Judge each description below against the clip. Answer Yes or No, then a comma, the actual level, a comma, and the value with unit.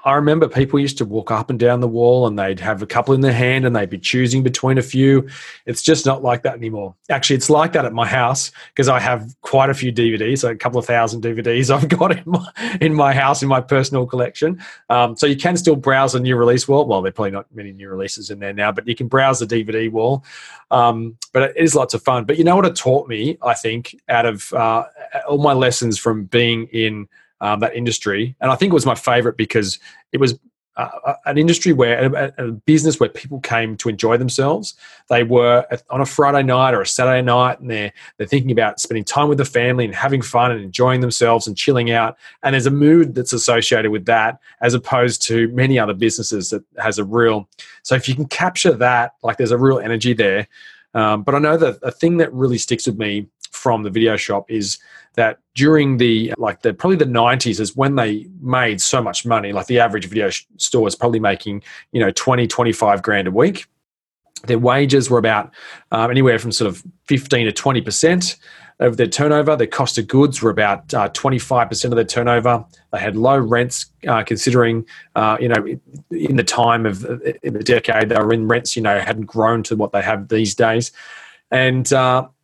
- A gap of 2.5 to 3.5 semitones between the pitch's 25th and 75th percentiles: Yes, average, 3.1 semitones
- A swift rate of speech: Yes, fast, 225 wpm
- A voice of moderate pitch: No, low, 120 Hz